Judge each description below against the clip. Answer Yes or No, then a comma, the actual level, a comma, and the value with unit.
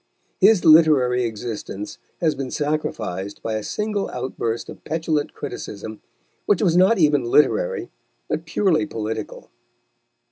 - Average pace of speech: No, slow, 120 wpm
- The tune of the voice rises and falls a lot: Yes, wide, 6.8 semitones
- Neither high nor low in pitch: Yes, medium, 145 Hz